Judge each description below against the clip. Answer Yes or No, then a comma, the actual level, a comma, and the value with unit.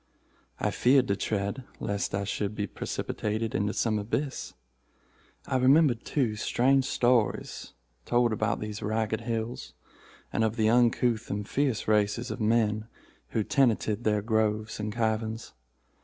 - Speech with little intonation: Yes, narrow, 2.3 semitones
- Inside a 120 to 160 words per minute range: Yes, average, 140 wpm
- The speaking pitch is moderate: No, low, 110 Hz